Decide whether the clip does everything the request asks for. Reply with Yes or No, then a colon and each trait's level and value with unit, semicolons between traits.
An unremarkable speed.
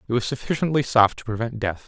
No: fast, 225 wpm